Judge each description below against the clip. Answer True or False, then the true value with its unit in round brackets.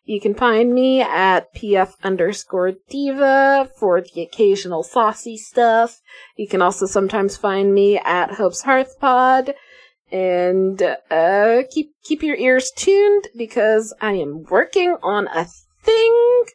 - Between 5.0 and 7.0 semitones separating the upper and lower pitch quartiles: True (5.6 semitones)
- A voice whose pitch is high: True (220 Hz)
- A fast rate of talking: False (135 wpm)